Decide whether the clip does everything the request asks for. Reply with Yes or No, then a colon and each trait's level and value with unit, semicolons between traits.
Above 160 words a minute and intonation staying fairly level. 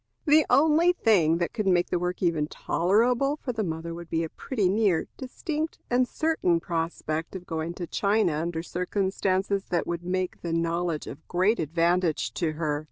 No: average, 175 wpm; average, 4.3 semitones